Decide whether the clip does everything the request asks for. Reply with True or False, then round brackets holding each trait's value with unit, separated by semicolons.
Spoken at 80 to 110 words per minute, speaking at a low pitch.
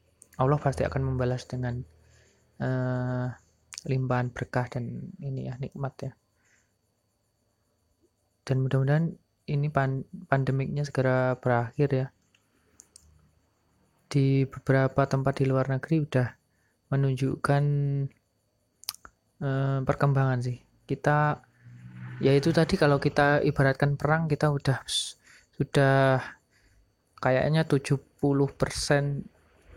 True (90 wpm; 130 Hz)